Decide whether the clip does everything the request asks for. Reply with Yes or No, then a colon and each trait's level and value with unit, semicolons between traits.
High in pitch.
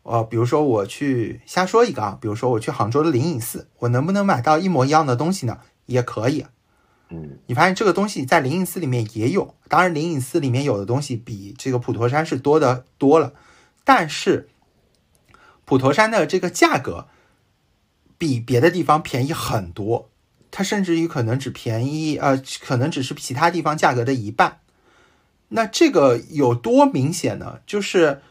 No: medium, 140 Hz